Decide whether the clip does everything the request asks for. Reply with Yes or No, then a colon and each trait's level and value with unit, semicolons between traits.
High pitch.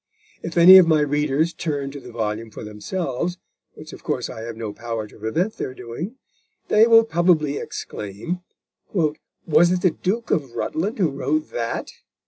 No: medium, 150 Hz